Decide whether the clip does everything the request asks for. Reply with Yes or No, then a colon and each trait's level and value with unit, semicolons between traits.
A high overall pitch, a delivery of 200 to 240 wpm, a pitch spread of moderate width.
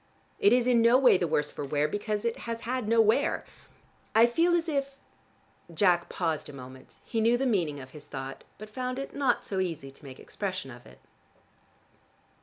No: high, 210 Hz; fast, 205 wpm; wide, 8.8 semitones